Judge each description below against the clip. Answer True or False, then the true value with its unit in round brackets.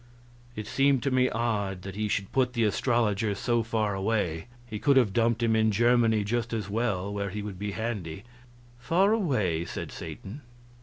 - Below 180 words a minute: False (185 wpm)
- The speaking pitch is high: False (110 Hz)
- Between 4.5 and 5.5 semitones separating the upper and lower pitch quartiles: False (3.0 semitones)